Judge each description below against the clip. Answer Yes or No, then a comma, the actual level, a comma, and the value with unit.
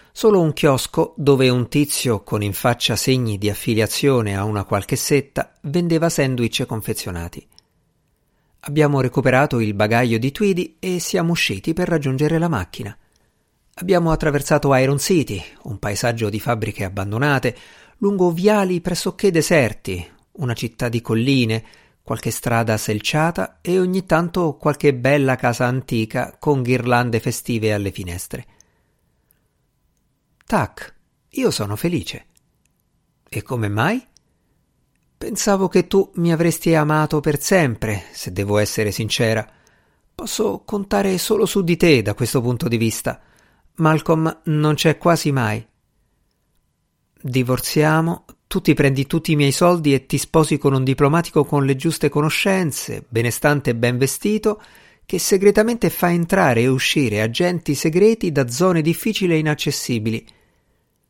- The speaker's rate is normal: Yes, average, 130 wpm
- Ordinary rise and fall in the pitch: No, wide, 6.4 semitones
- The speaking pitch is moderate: Yes, medium, 145 Hz